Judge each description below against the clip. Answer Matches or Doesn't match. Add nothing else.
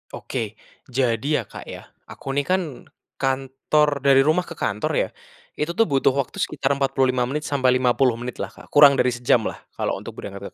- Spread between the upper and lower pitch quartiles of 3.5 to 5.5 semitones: Doesn't match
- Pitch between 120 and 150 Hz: Matches